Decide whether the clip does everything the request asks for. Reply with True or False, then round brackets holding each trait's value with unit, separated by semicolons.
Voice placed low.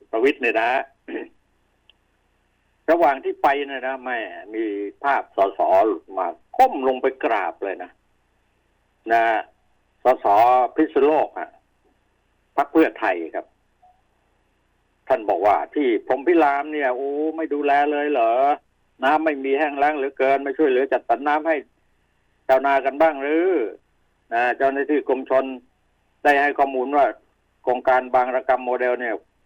False (145 Hz)